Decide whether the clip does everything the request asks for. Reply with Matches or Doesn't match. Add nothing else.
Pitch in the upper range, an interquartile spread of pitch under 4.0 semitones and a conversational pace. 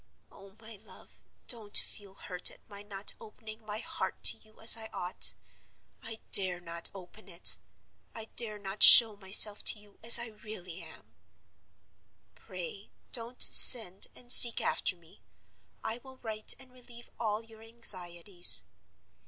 Matches